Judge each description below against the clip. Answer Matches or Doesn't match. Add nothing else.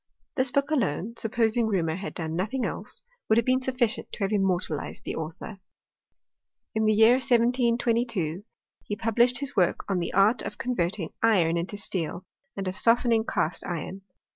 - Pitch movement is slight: Doesn't match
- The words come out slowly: Doesn't match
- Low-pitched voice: Doesn't match